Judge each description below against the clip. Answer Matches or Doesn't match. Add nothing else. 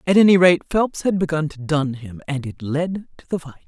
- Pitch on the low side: Doesn't match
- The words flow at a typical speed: Doesn't match